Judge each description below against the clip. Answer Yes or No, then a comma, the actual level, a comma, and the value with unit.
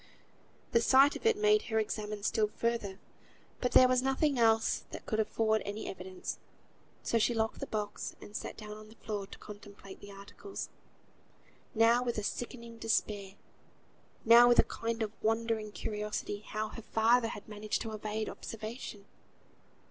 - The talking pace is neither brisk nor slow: Yes, average, 165 wpm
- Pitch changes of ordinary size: No, narrow, 1.8 semitones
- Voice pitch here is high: Yes, high, 220 Hz